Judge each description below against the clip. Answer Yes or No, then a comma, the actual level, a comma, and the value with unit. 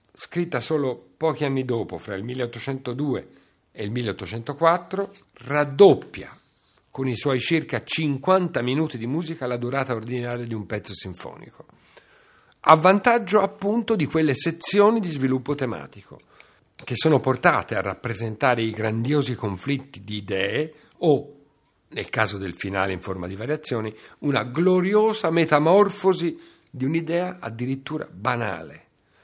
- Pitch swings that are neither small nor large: No, wide, 6.0 semitones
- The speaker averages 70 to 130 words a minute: Yes, average, 125 wpm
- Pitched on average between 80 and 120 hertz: No, low, 135 Hz